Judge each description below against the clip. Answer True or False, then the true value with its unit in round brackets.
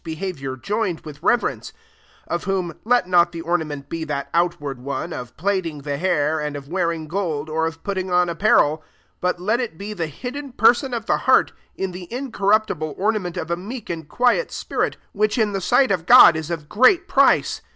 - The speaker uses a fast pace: False (185 wpm)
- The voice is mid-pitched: True (175 Hz)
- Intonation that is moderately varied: True (4.8 semitones)